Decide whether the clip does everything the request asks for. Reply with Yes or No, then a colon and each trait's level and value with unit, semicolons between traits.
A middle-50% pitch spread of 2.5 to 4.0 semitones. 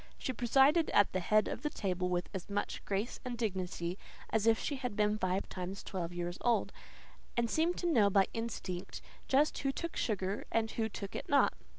No: average, 4.6 semitones